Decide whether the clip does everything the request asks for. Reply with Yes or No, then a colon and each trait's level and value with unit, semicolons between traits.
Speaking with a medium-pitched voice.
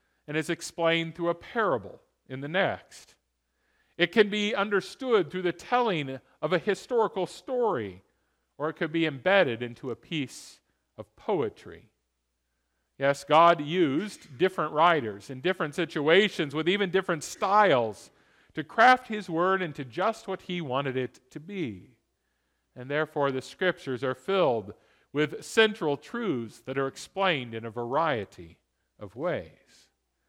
Yes: medium, 160 Hz